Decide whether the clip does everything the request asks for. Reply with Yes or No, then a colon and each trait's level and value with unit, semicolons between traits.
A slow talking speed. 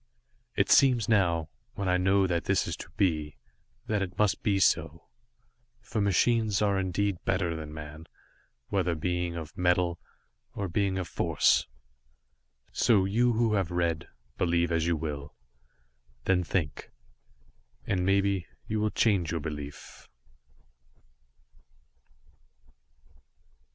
Yes: slow, 125 wpm